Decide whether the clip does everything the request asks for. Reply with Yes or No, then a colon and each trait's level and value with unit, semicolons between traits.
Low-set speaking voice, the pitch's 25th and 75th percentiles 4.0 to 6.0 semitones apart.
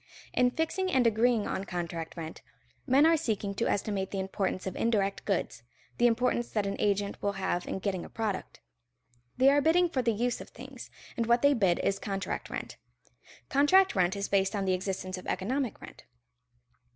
No: high, 205 Hz; average, 4.5 semitones